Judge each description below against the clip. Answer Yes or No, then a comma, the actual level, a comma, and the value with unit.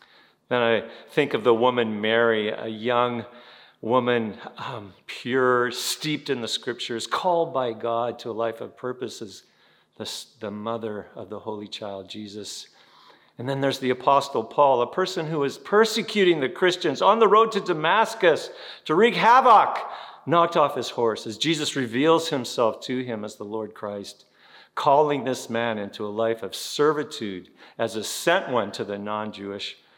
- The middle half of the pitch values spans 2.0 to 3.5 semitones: No, average, 5.1 semitones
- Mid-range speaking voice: No, low, 125 Hz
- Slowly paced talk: No, average, 165 wpm